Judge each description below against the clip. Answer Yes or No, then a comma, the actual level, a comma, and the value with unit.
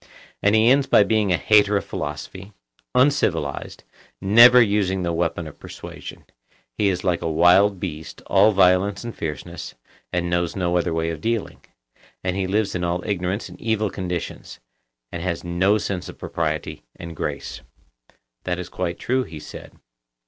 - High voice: No, very low, 95 Hz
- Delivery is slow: No, average, 165 wpm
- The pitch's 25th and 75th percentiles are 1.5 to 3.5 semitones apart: Yes, average, 3.1 semitones